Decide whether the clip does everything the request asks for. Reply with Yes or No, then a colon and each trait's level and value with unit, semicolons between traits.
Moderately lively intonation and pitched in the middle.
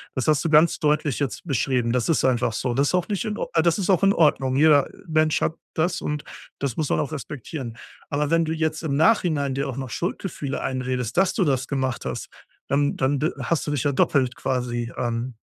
Yes: average, 3.6 semitones; medium, 145 Hz